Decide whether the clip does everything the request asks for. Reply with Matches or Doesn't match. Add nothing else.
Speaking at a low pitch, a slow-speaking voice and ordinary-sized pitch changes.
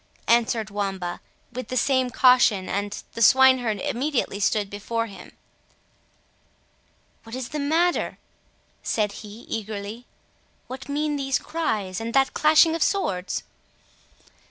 Doesn't match